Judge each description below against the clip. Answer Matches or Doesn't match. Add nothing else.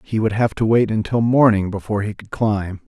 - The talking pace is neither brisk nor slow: Doesn't match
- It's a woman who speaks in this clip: Doesn't match